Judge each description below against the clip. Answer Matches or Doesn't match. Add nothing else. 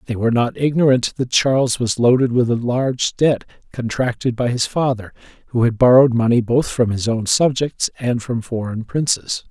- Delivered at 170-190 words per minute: Matches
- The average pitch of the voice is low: Matches